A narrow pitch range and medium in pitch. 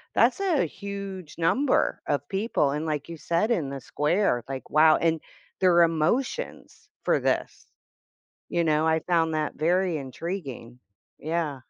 No: average, 3.7 semitones; medium, 165 Hz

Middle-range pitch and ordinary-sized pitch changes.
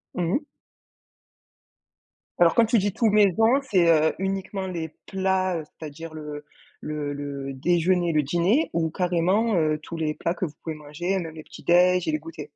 Yes: medium, 170 Hz; average, 3.5 semitones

